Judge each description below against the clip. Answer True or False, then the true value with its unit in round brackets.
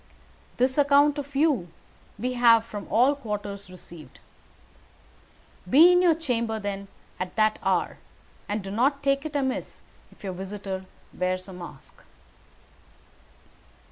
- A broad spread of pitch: True (6.3 semitones)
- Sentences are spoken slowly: True (130 wpm)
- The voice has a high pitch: True (225 Hz)